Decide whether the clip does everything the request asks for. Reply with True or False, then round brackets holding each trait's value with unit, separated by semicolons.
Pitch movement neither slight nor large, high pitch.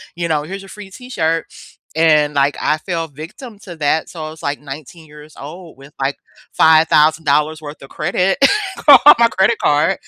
False (3.6 semitones; 160 Hz)